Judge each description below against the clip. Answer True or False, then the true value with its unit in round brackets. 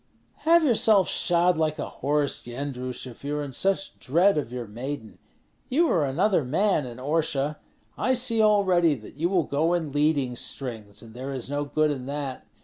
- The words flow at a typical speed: True (185 wpm)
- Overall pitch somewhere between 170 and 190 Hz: False (145 Hz)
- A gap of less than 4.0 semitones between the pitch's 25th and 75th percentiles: False (5.3 semitones)